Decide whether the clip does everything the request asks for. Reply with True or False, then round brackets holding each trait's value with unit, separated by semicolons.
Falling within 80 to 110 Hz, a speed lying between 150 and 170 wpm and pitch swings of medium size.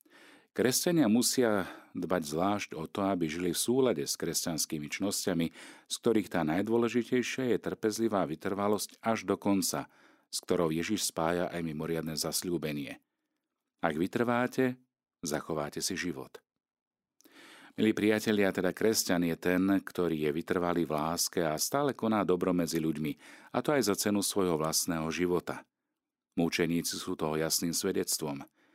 False (90 Hz; 135 wpm; 5.0 semitones)